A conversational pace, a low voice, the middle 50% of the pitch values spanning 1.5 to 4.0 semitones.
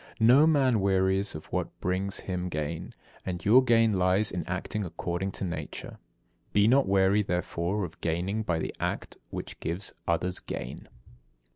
Yes: average, 160 wpm; very low, 95 Hz; average, 3.2 semitones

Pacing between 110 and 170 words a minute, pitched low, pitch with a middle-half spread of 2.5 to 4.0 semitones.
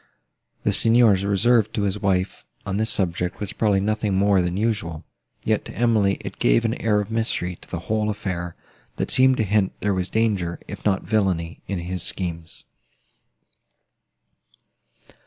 Yes: average, 160 wpm; low, 100 Hz; average, 3.0 semitones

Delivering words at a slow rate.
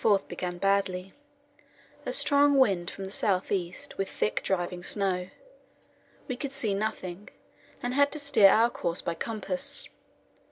No: average, 155 wpm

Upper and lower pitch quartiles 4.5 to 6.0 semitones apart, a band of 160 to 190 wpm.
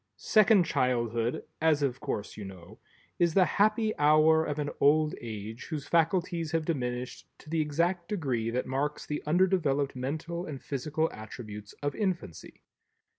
No: average, 5.1 semitones; average, 150 wpm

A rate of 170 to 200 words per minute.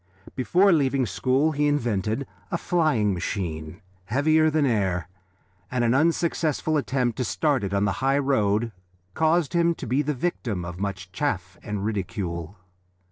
No: average, 150 wpm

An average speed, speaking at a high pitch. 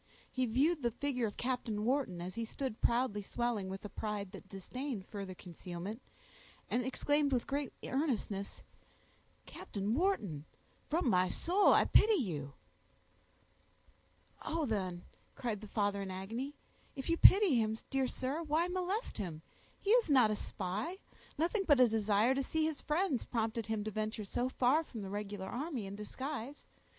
Yes: average, 160 wpm; high, 235 Hz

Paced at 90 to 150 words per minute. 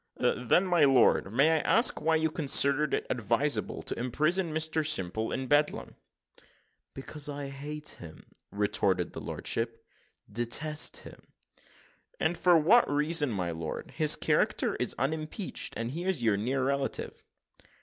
Yes: average, 145 wpm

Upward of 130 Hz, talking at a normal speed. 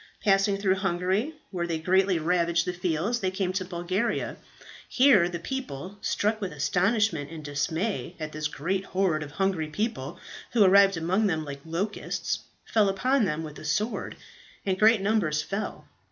Yes: medium, 185 Hz; average, 165 wpm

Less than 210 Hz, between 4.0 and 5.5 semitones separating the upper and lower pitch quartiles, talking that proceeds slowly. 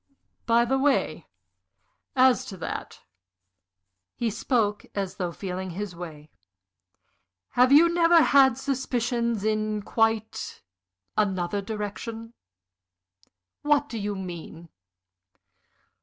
No: high, 220 Hz; average, 4.7 semitones; slow, 95 wpm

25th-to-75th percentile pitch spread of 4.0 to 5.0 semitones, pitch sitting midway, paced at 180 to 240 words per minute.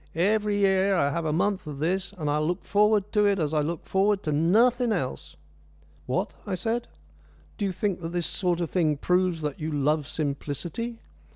Yes: average, 4.7 semitones; medium, 180 Hz; average, 195 wpm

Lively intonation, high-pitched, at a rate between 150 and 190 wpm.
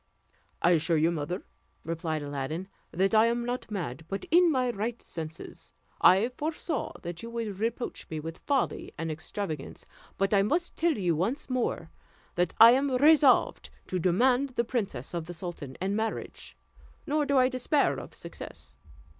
Yes: wide, 7.2 semitones; high, 205 Hz; average, 165 wpm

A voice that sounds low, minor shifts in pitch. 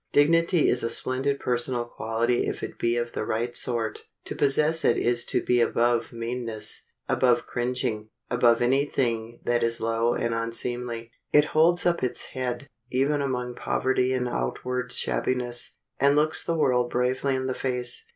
Yes: low, 125 Hz; narrow, 1.9 semitones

